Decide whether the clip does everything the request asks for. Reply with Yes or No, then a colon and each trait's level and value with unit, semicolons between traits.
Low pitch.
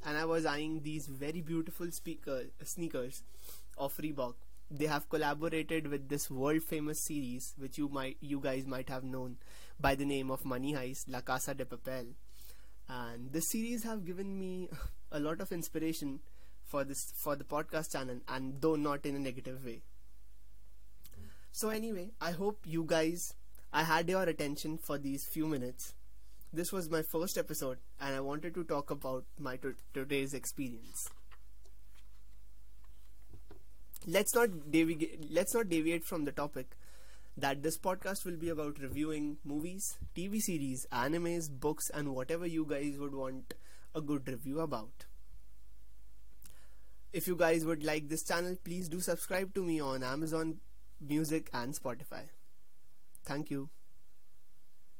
No: medium, 145 Hz